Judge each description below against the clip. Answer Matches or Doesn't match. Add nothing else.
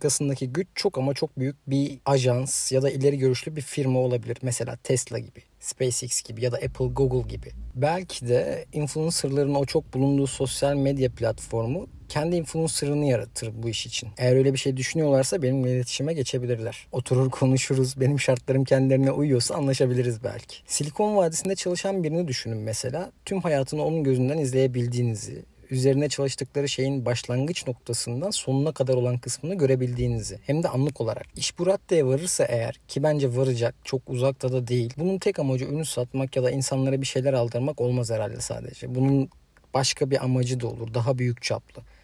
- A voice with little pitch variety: Matches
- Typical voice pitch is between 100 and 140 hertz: Matches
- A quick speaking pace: Matches